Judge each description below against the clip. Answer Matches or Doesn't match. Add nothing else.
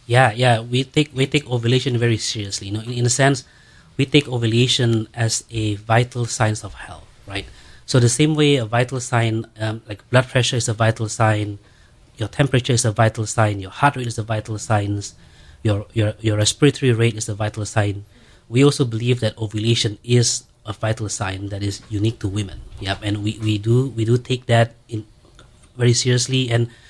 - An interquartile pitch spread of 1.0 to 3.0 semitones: Matches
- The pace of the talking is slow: Doesn't match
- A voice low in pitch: Matches